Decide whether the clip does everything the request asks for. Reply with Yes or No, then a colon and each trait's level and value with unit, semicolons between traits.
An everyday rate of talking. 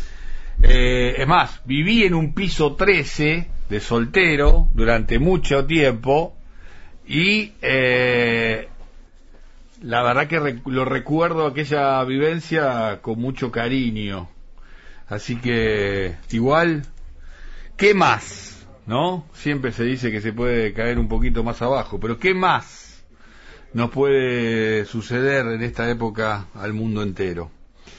No: slow, 120 wpm